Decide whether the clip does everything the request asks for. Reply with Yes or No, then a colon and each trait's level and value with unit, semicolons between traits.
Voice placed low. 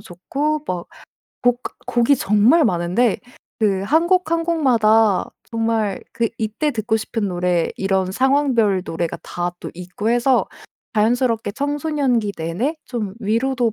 No: high, 225 Hz